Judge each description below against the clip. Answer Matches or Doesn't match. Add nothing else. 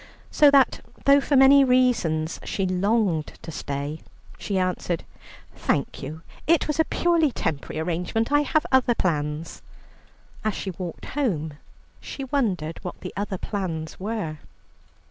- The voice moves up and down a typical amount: Doesn't match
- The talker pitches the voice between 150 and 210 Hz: Matches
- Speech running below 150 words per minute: Matches